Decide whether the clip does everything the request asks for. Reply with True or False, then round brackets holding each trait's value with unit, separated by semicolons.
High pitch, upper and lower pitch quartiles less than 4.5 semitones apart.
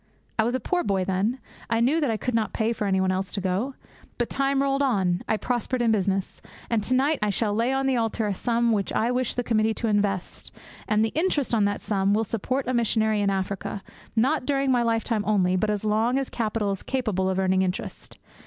True (220 Hz; 3.9 semitones)